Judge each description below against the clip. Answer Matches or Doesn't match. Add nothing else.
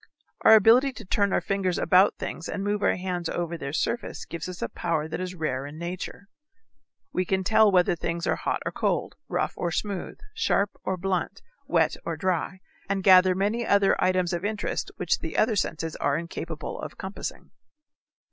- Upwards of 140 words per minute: Matches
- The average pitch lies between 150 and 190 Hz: Matches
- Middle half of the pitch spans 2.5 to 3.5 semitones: Matches